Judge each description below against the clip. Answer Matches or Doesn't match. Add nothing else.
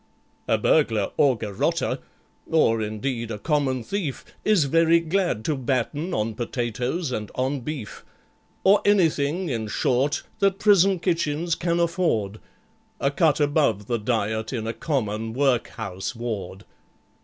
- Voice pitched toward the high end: Doesn't match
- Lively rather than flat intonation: Matches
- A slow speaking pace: Matches